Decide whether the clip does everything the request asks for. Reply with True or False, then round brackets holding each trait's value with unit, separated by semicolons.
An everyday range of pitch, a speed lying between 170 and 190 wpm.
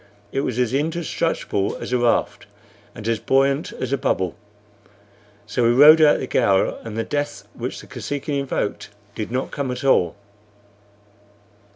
False (4.0 semitones; 160 wpm)